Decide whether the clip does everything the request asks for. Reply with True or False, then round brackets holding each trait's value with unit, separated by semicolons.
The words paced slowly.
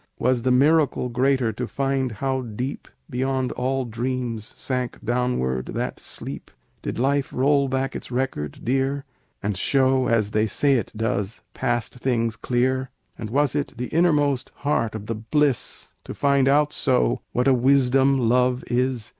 False (155 wpm)